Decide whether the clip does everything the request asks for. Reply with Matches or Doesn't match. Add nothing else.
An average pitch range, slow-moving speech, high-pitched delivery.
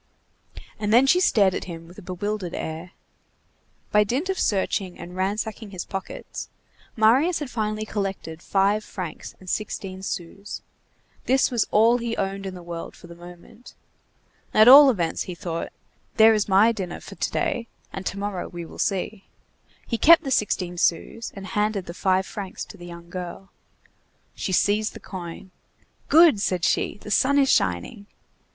Doesn't match